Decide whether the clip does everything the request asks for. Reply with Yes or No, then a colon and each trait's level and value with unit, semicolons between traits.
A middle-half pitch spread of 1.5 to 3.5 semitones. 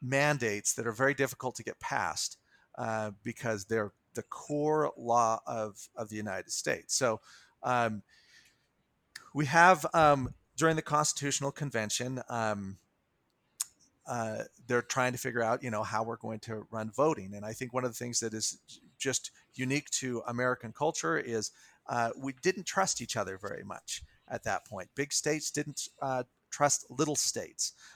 No: average, 4.2 semitones